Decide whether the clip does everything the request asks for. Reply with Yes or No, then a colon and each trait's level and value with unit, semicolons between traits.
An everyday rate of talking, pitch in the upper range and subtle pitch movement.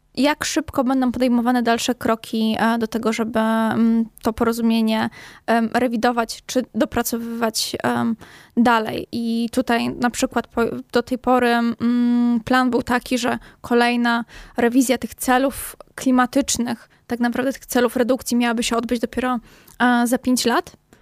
Yes: average, 125 wpm; high, 240 Hz; narrow, 1.5 semitones